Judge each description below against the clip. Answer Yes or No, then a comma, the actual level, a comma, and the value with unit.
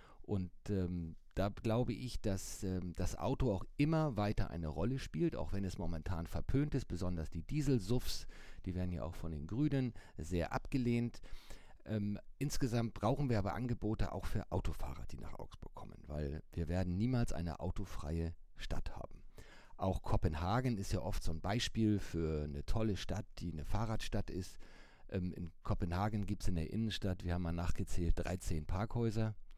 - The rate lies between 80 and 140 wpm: No, average, 170 wpm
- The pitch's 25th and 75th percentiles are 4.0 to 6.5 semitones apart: Yes, average, 4.7 semitones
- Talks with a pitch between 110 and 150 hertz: No, very low, 95 Hz